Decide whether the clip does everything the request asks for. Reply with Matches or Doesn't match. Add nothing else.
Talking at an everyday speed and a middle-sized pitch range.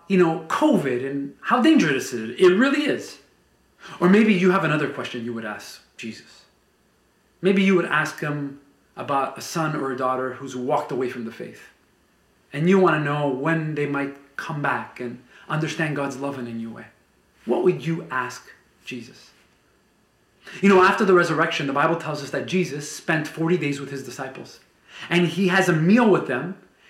Matches